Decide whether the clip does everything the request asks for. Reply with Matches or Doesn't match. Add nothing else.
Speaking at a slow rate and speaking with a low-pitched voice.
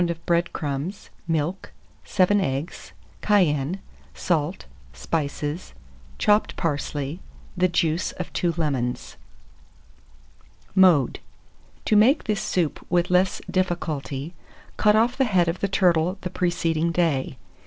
Doesn't match